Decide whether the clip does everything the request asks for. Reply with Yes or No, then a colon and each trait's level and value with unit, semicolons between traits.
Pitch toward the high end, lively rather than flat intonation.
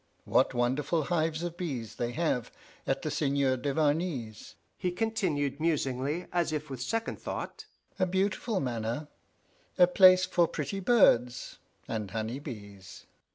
No: medium, 150 Hz; wide, 6.1 semitones